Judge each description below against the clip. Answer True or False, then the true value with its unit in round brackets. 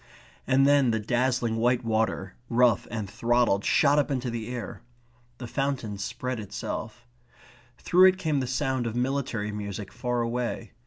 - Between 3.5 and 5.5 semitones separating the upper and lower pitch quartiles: False (2.9 semitones)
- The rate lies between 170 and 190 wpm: False (155 wpm)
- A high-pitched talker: False (120 Hz)